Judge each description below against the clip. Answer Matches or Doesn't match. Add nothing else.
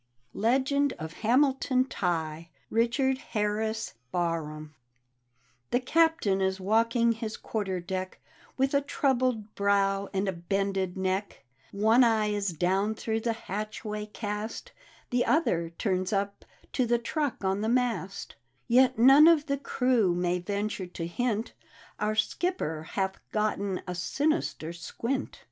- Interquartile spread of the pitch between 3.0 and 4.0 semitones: Doesn't match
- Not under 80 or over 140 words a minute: Matches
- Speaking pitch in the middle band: Doesn't match